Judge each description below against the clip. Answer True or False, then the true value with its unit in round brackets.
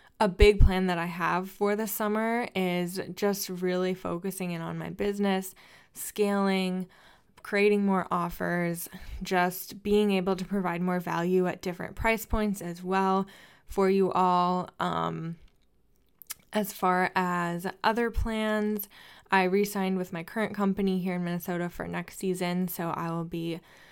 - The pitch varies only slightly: True (2.2 semitones)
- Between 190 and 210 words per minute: False (150 wpm)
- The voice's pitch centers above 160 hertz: True (185 Hz)